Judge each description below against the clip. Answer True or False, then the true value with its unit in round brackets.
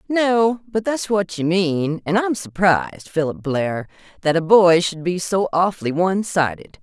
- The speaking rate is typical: True (175 wpm)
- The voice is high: False (180 Hz)